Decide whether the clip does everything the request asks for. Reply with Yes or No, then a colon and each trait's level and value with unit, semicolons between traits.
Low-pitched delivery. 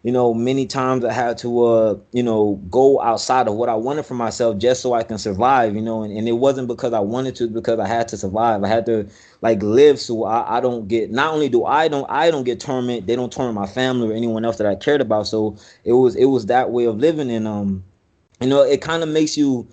Yes: low, 120 Hz